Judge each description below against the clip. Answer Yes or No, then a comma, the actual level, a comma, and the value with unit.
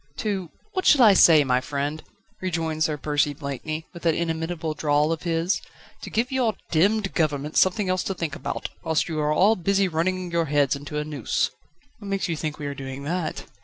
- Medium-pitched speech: Yes, medium, 160 Hz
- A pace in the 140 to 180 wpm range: No, average, 200 wpm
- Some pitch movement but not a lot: Yes, average, 3.8 semitones